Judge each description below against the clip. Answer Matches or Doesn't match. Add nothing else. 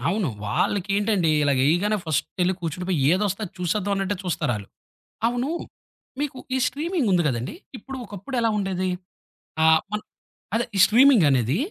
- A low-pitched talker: Doesn't match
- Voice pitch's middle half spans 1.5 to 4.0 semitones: Doesn't match